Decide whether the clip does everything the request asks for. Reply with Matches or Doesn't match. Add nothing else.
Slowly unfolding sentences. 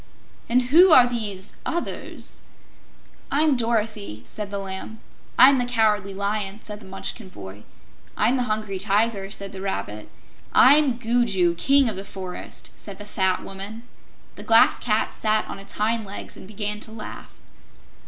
Doesn't match